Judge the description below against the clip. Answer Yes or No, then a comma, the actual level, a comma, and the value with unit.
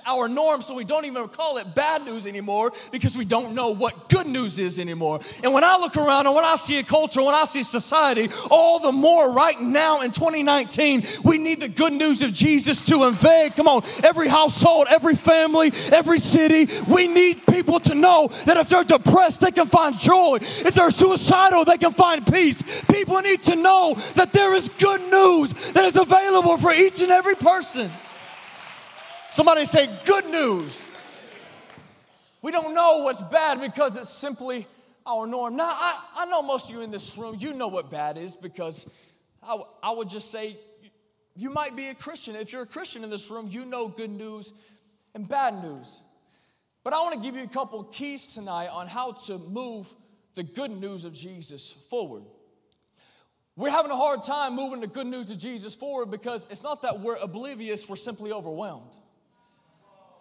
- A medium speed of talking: Yes, average, 190 wpm